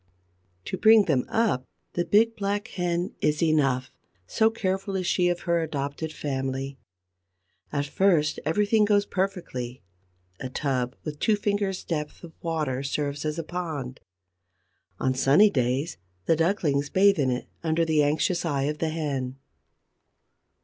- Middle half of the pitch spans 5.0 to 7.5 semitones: Yes, average, 5.3 semitones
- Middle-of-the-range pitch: Yes, medium, 160 Hz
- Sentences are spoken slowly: No, average, 145 wpm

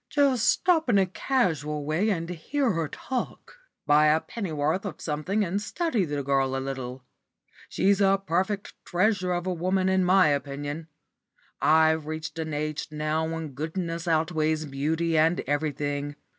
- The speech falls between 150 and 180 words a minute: Yes, average, 155 wpm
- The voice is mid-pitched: Yes, medium, 160 Hz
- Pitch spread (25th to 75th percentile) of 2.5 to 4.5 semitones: Yes, average, 4.0 semitones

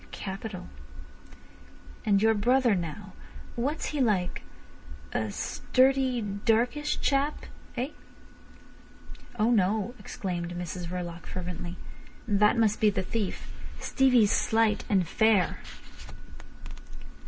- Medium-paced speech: No, slow, 90 wpm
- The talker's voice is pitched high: Yes, high, 210 Hz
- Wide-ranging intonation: No, average, 4.7 semitones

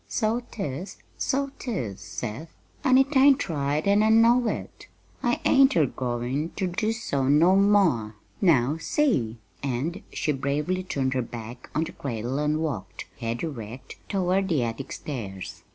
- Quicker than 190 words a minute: No, average, 155 wpm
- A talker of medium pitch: Yes, medium, 150 Hz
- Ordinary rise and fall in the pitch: No, wide, 8.4 semitones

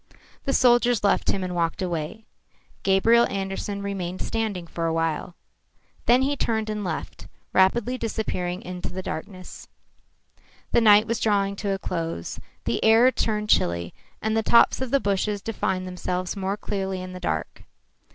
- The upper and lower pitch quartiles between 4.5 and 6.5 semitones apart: No, average, 3.5 semitones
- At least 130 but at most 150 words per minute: No, average, 160 wpm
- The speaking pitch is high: Yes, high, 195 Hz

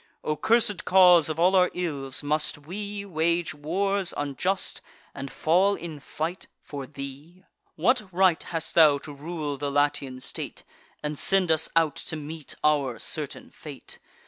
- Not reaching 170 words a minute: Yes, average, 150 wpm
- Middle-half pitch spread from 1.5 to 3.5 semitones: No, average, 4.0 semitones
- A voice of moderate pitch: Yes, medium, 160 Hz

